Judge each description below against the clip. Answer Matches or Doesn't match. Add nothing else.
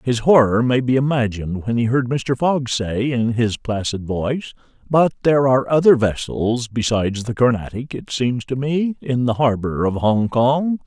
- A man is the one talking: Matches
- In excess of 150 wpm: Matches